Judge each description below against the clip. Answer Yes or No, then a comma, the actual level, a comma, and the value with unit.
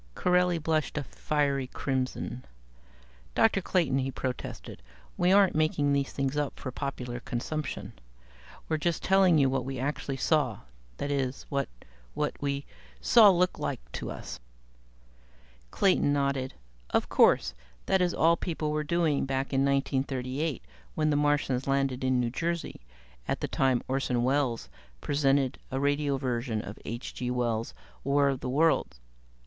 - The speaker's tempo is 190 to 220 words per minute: No, average, 150 wpm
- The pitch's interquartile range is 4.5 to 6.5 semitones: No, average, 2.8 semitones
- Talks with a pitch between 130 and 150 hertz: Yes, medium, 140 Hz